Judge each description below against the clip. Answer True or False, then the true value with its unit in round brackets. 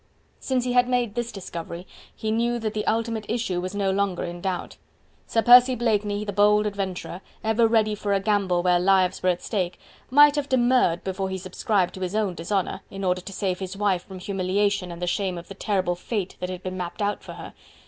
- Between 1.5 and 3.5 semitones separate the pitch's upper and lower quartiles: True (3.1 semitones)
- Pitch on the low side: False (200 Hz)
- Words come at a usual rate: False (220 wpm)